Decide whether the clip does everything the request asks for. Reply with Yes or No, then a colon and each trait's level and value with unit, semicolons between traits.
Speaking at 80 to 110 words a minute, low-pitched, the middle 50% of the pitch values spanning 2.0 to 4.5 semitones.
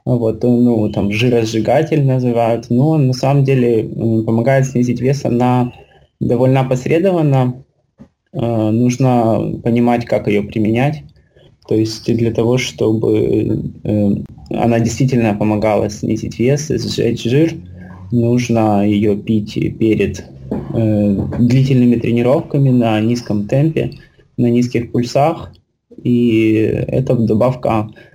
Yes: slow, 105 wpm; low, 115 Hz; narrow, 2.4 semitones